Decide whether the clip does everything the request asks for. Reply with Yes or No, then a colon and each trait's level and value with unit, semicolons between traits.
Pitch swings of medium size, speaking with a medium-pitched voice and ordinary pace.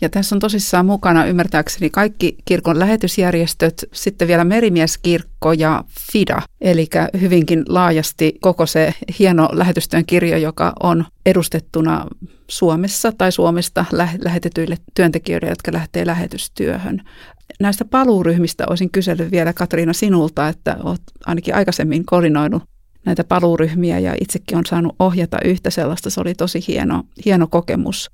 No: narrow, 1.9 semitones; medium, 175 Hz; average, 130 wpm